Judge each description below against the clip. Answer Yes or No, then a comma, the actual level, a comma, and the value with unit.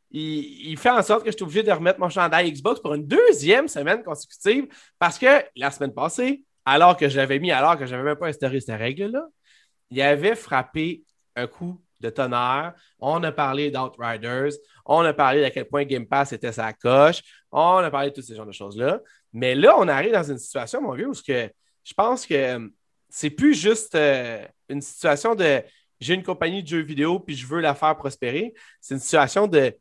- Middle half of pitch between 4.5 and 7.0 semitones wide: Yes, wide, 5.4 semitones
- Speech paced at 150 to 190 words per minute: No, average, 210 wpm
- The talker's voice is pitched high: No, medium, 150 Hz